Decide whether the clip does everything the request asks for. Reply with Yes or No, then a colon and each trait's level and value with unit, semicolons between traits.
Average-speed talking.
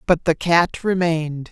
Yes: average, 160 wpm